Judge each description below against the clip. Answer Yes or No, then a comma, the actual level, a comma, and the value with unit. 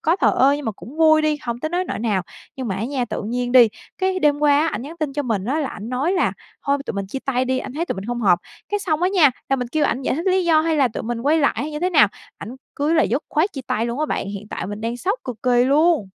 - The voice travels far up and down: No, average, 4.8 semitones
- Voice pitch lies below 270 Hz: No, very high, 275 Hz